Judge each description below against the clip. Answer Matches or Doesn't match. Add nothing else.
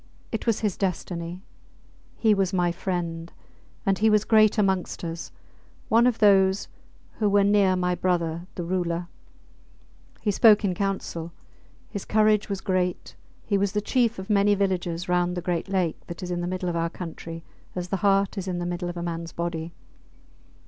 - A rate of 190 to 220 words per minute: Doesn't match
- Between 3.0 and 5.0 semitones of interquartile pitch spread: Doesn't match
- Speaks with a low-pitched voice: Doesn't match